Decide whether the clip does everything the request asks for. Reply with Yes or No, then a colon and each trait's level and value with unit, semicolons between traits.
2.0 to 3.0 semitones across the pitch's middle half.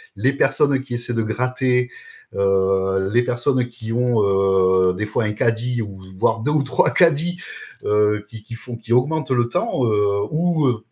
No: average, 3.4 semitones